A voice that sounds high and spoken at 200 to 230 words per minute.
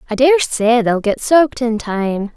Yes: high, 240 Hz; fast, 205 wpm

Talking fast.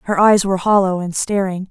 Yes: fast, 210 wpm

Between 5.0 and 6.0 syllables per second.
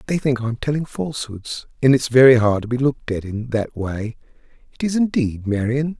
Yes: 5.3 syllables/s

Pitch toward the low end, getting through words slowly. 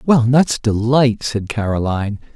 Yes: low, 115 Hz; slow, 125 wpm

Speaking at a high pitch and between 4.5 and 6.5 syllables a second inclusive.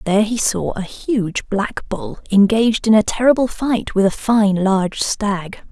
No: high, 210 Hz; 4.3 syllables/s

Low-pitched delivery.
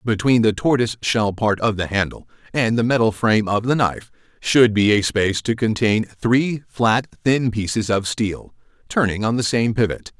Yes: low, 110 Hz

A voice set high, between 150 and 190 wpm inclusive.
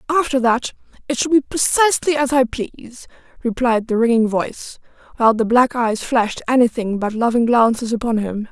Yes: high, 245 Hz; average, 170 wpm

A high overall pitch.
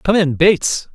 No: medium, 170 Hz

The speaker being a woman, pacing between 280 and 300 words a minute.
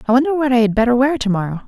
Yes: female; fast, 285 wpm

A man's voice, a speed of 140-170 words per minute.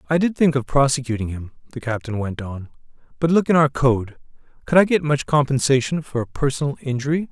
No: male; average, 195 wpm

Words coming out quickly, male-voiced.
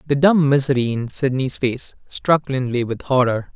No: average, 170 wpm; male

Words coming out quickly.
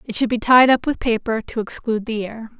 Yes: fast, 255 wpm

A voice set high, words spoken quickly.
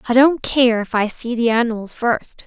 Yes: high, 235 Hz; fast, 220 wpm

